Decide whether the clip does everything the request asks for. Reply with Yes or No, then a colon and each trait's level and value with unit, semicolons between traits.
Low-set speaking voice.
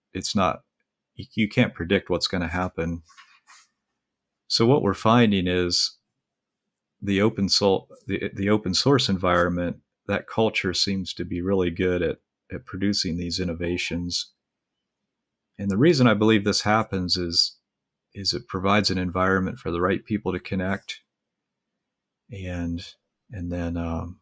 Yes: very low, 95 Hz